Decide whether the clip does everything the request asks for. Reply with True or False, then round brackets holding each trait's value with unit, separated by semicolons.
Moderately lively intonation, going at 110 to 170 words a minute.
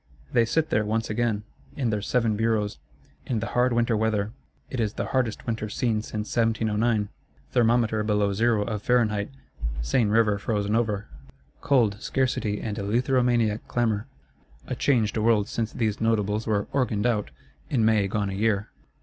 False (2.1 semitones; 160 wpm)